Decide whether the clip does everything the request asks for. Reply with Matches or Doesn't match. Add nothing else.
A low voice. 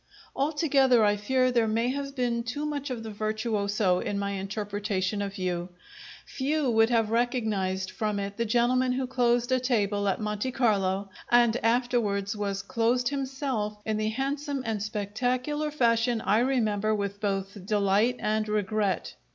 Doesn't match